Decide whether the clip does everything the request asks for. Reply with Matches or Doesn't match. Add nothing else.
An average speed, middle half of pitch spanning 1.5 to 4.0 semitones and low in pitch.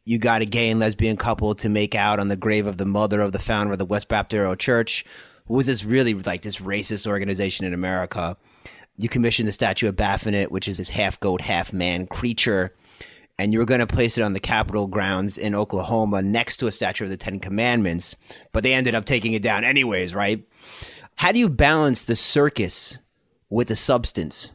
Doesn't match